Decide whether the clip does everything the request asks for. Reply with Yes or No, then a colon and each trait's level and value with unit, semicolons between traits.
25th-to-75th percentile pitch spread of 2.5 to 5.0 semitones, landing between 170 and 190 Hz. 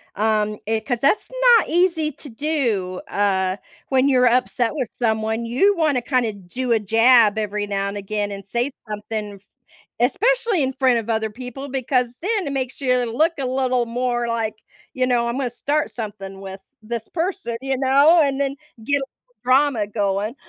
No: average, 4.1 semitones; high, 245 Hz